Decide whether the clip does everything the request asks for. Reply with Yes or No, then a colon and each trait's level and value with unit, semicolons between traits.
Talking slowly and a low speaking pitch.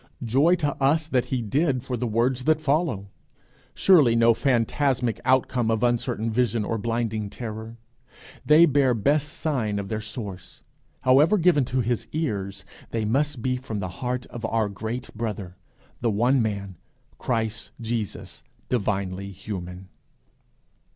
No: average, 145 wpm; low, 115 Hz